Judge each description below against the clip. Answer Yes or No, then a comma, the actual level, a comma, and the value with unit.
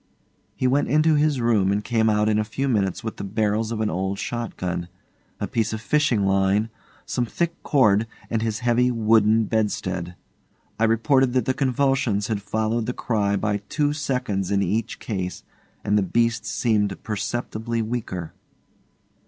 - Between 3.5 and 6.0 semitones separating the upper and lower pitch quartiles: No, average, 3.1 semitones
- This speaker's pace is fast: No, average, 170 wpm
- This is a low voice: Yes, low, 110 Hz